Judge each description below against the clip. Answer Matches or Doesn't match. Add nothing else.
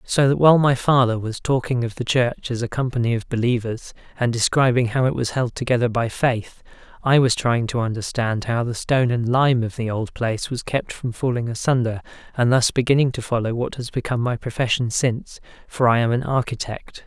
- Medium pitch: Doesn't match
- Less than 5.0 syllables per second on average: Doesn't match